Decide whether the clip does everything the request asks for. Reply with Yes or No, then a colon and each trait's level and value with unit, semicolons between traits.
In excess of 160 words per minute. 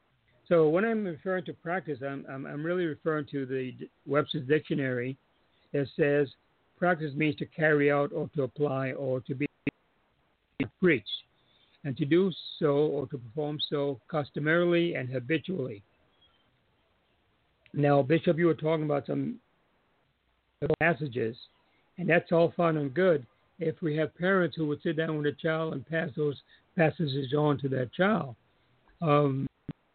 No: average, 150 wpm